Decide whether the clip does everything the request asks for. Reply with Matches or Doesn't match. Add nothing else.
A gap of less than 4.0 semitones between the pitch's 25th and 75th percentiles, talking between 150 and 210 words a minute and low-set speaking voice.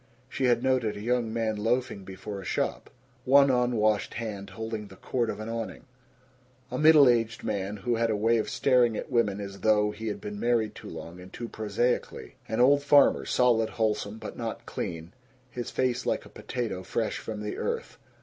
Matches